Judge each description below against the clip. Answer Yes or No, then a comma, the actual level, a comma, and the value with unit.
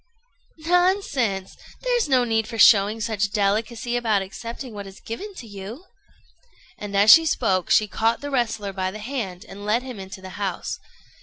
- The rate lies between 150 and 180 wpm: Yes, average, 170 wpm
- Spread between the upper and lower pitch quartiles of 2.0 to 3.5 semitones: No, average, 3.9 semitones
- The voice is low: No, high, 220 Hz